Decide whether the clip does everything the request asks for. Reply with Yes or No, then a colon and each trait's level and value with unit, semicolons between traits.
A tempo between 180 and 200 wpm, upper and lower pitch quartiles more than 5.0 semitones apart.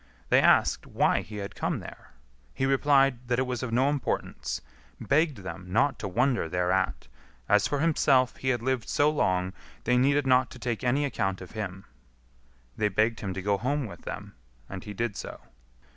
Yes: average, 190 wpm; wide, 5.5 semitones